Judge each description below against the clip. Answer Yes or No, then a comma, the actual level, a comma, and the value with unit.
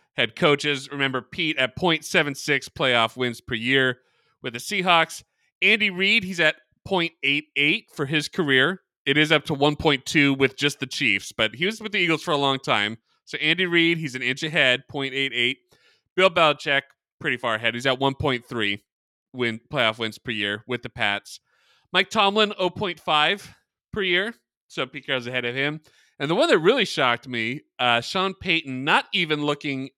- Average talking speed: Yes, average, 175 wpm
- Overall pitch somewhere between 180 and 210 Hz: No, medium, 145 Hz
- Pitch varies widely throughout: No, average, 4.8 semitones